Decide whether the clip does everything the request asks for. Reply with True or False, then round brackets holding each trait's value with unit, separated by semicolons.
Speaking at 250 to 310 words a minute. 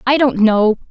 False (200 wpm)